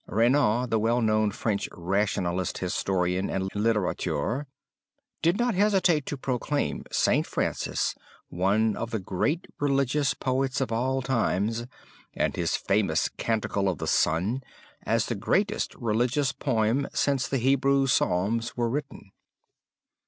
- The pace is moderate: No, slow, 130 wpm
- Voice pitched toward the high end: No, low, 115 Hz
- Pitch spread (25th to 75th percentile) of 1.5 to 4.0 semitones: No, average, 5.1 semitones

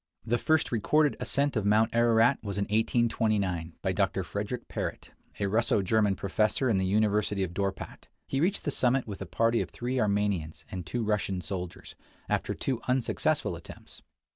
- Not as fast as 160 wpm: No, average, 175 wpm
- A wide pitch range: No, average, 3.5 semitones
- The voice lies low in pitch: Yes, low, 105 Hz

